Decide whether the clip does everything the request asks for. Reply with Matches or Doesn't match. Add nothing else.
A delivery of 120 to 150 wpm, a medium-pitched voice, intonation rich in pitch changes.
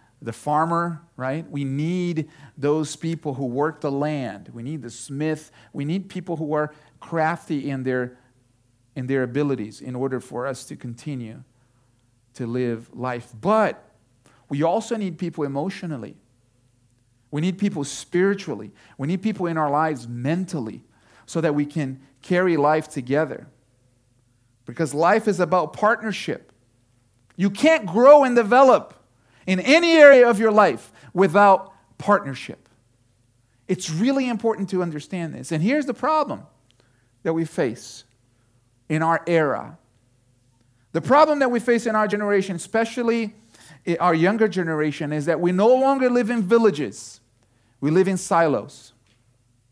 Matches